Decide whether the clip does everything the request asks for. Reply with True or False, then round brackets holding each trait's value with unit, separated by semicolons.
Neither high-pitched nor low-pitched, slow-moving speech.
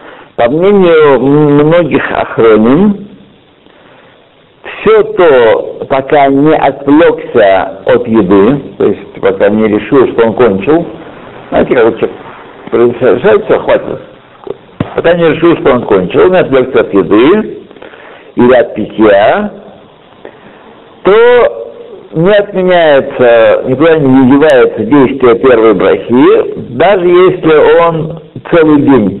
True (170 Hz; 100 wpm)